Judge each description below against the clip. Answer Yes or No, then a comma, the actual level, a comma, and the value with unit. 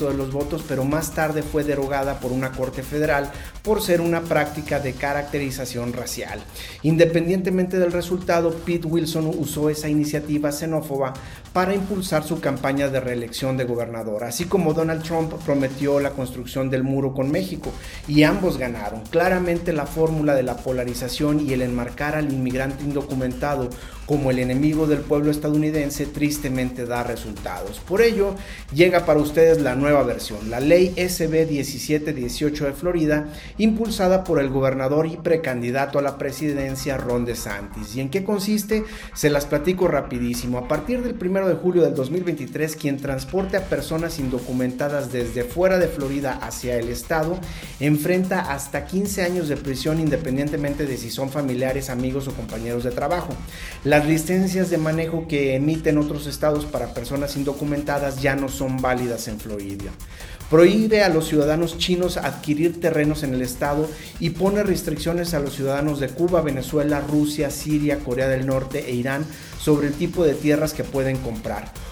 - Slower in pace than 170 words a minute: Yes, average, 160 wpm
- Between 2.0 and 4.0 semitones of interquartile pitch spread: Yes, average, 3.7 semitones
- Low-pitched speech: No, medium, 145 Hz